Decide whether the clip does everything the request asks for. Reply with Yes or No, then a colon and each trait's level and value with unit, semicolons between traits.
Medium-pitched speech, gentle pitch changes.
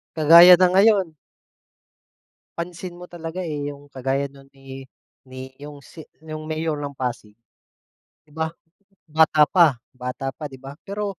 No: medium, 150 Hz; average, 3.7 semitones